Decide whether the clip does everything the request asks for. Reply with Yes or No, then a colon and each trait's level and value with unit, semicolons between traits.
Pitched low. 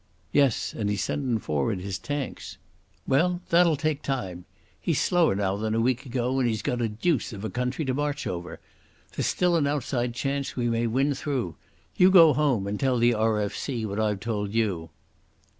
Yes: low, 120 Hz